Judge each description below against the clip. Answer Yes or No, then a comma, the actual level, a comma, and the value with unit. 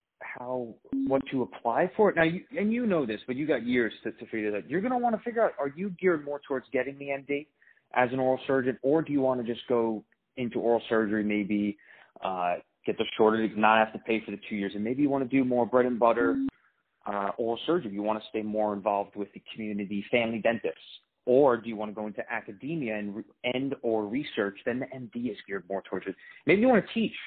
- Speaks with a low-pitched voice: Yes, low, 120 Hz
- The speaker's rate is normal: No, fast, 245 wpm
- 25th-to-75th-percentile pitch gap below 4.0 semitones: No, average, 4.3 semitones